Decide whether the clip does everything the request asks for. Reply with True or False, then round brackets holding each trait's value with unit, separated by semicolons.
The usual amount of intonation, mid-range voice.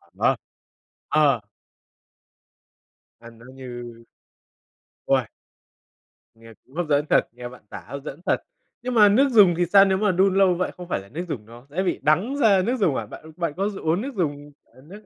False (7.1 semitones; 165 Hz)